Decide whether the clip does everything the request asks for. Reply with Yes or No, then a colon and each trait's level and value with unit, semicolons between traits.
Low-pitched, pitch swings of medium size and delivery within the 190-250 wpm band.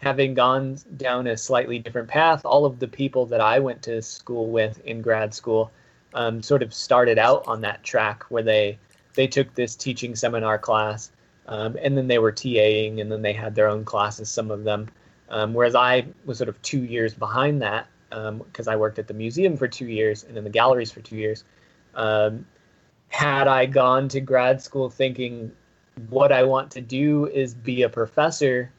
Yes: low, 120 Hz; average, 3.3 semitones; average, 200 wpm